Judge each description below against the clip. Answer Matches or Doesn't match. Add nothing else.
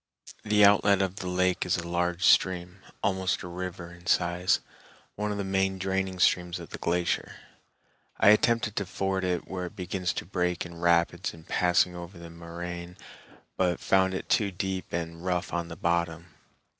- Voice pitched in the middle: Doesn't match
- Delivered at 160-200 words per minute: Matches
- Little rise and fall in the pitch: Matches